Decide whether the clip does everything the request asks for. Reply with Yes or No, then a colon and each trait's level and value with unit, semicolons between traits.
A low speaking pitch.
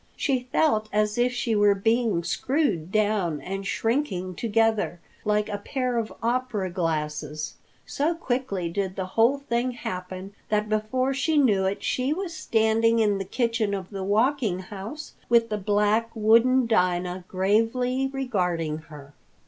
No: high, 215 Hz